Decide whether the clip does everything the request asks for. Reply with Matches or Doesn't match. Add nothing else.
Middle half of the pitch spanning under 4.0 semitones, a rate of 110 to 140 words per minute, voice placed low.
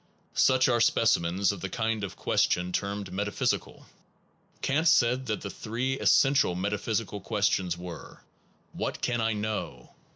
Matches